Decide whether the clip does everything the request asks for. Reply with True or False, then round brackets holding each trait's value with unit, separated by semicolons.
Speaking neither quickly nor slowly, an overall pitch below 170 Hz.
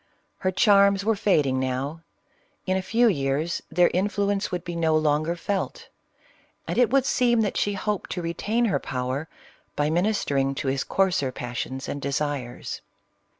False (165 wpm; 175 Hz)